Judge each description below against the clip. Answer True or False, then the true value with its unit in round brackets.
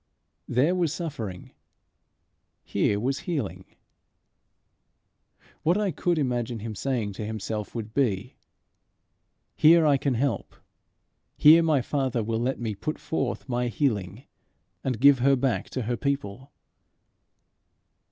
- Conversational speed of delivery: False (125 wpm)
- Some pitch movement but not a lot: True (4.4 semitones)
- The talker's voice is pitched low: True (125 Hz)